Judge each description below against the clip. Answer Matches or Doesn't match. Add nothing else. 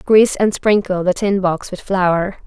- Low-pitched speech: Doesn't match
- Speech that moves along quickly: Doesn't match